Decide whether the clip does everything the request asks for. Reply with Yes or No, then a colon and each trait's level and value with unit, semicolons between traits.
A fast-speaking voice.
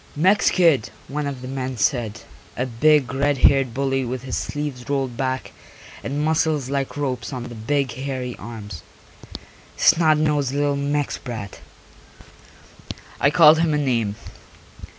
No: average, 145 wpm